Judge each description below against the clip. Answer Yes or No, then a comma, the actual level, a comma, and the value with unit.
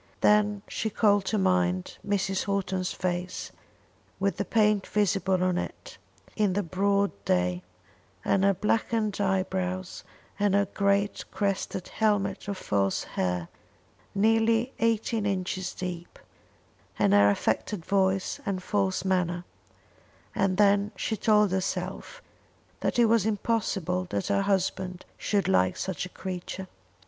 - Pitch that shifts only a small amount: Yes, narrow, 2.1 semitones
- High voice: Yes, high, 195 Hz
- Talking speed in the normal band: No, slow, 130 wpm